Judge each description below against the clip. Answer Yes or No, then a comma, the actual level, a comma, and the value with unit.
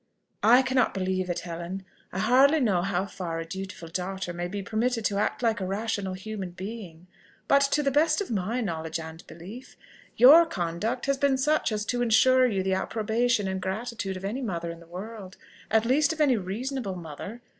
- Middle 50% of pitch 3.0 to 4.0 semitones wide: No, average, 5.1 semitones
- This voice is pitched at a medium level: No, high, 205 Hz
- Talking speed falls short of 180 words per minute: No, average, 195 wpm